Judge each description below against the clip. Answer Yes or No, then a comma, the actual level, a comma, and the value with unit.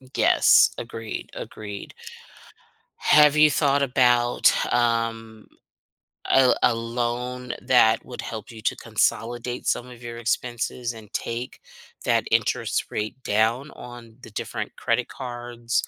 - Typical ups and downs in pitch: No, narrow, 1.5 semitones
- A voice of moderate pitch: No, low, 120 Hz